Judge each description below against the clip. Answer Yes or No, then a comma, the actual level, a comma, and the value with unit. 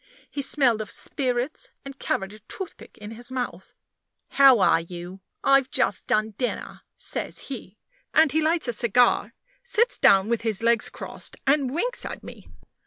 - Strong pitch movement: No, average, 4.6 semitones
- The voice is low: No, very high, 250 Hz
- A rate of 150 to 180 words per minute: Yes, average, 165 wpm